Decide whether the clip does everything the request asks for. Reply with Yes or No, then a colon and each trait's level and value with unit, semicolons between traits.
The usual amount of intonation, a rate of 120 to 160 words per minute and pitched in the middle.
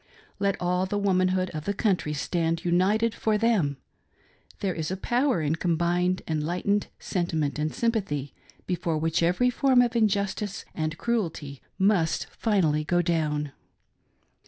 Yes: average, 4.2 semitones; average, 140 wpm; medium, 180 Hz